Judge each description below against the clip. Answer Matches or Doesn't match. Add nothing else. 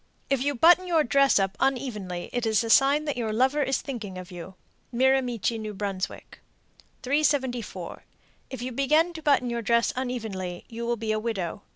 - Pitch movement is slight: Doesn't match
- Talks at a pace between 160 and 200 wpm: Matches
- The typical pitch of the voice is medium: Doesn't match